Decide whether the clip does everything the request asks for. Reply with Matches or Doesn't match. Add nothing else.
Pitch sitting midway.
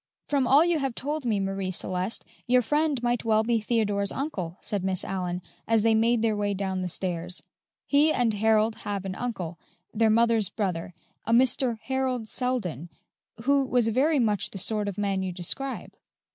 Doesn't match